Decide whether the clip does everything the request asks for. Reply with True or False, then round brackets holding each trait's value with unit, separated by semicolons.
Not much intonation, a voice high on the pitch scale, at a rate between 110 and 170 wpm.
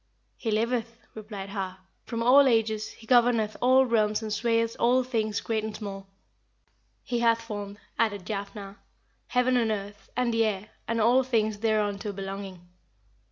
True (2.3 semitones; 220 Hz; 155 wpm)